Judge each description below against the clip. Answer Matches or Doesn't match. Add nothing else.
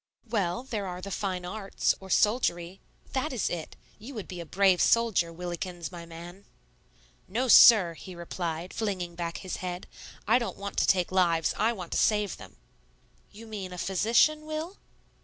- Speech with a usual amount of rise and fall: Matches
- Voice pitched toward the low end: Doesn't match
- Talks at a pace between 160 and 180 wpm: Matches